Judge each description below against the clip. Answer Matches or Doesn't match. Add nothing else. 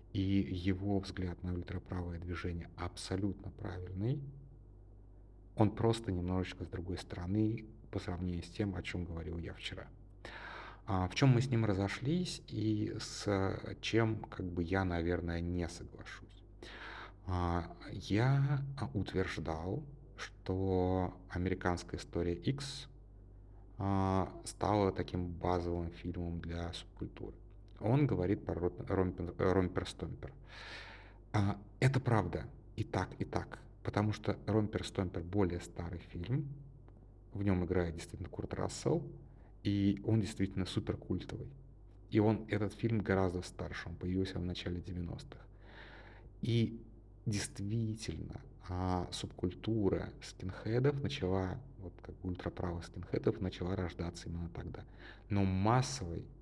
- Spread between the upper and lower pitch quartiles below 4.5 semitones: Matches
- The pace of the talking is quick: Doesn't match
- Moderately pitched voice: Doesn't match